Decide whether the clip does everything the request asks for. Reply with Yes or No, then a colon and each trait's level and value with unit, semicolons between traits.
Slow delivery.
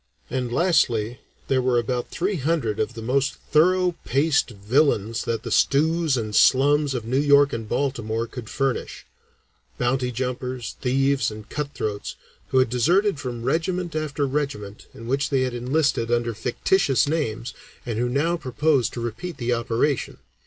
No: average, 160 wpm